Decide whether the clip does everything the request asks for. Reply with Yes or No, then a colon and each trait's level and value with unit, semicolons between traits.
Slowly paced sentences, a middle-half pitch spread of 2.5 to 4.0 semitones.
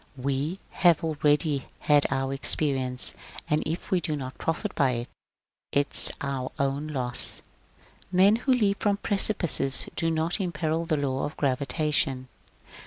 No: average, 145 wpm; average, 3.7 semitones